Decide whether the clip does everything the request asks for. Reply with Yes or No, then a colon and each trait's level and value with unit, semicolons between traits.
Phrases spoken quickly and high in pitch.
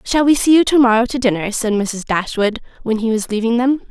Yes: fast, 230 wpm; high, 235 Hz